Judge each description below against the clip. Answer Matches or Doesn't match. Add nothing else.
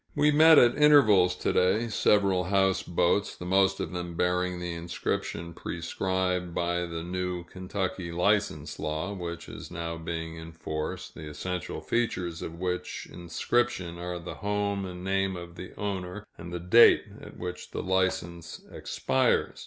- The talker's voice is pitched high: Doesn't match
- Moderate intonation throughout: Doesn't match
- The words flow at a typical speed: Matches